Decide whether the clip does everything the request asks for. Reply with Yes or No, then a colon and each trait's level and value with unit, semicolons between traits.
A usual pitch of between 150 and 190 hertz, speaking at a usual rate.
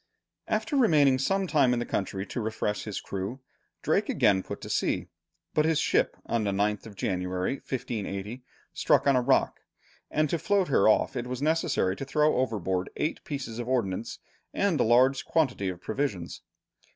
No: low, 125 Hz; average, 175 wpm